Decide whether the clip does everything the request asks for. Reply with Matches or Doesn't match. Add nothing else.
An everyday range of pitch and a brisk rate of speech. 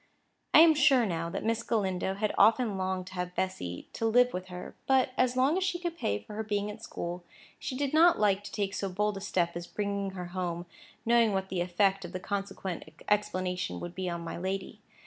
Matches